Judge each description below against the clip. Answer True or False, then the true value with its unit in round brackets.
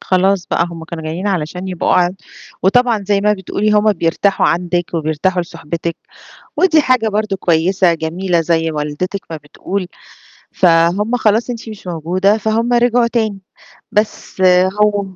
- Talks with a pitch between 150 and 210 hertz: True (190 Hz)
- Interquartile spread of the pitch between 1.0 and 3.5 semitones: False (4.0 semitones)